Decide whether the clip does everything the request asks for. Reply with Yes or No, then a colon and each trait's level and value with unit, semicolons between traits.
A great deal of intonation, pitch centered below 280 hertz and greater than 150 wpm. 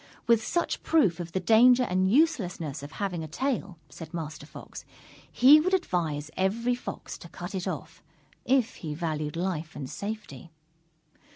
Yes: wide, 6.8 semitones; medium, 185 Hz; average, 160 wpm